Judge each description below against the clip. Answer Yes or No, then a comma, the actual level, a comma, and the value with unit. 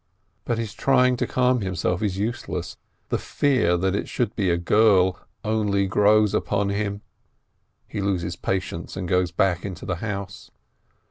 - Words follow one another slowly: No, average, 155 wpm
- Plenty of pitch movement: No, average, 2.8 semitones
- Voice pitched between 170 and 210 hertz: No, low, 100 Hz